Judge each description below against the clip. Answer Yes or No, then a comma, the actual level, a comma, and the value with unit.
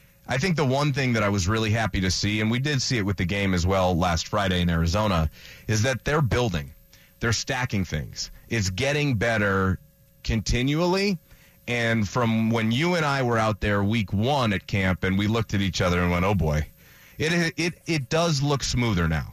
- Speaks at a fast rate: Yes, fast, 210 wpm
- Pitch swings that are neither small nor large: No, wide, 5.8 semitones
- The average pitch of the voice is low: Yes, low, 110 Hz